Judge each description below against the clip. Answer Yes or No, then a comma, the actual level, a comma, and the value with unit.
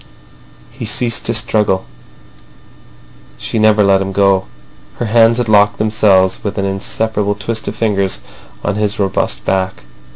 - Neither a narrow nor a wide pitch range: No, narrow, 2.1 semitones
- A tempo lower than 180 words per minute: Yes, average, 140 wpm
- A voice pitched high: No, low, 105 Hz